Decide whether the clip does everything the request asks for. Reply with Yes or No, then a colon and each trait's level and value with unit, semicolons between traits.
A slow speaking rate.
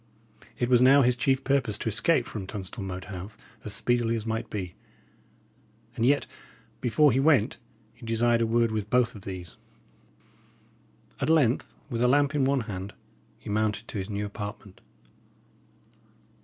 No: average, 160 wpm